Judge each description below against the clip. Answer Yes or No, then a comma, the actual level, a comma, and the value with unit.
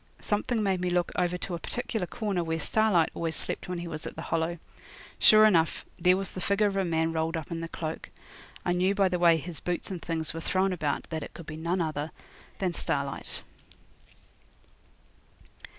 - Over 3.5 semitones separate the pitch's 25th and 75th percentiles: No, narrow, 2.6 semitones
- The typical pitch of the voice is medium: Yes, medium, 175 Hz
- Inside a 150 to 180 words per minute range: No, average, 200 wpm